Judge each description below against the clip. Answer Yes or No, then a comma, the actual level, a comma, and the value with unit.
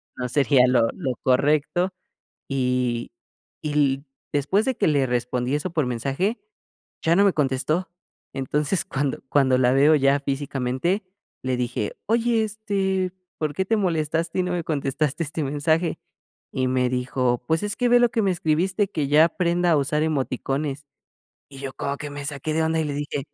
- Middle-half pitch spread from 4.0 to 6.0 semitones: Yes, average, 4.5 semitones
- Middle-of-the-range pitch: Yes, medium, 145 Hz